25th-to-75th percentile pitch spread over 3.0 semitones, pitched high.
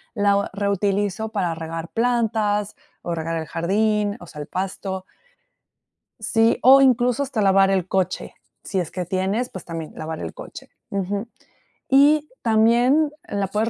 Yes: average, 3.5 semitones; high, 200 Hz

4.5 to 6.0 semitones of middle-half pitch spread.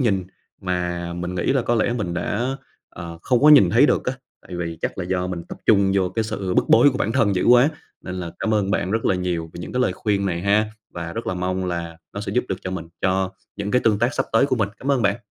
No: average, 3.9 semitones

